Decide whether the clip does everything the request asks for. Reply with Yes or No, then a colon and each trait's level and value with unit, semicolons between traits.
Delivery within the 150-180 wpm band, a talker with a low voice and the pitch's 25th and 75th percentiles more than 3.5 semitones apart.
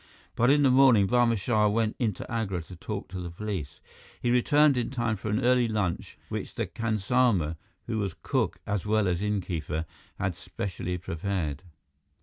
Yes: average, 170 wpm; low, 105 Hz; average, 4.7 semitones